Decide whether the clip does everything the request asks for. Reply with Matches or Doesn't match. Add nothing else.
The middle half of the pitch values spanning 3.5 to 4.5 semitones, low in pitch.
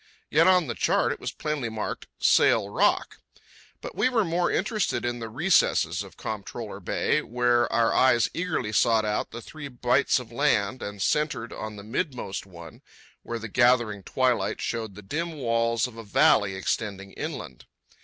Doesn't match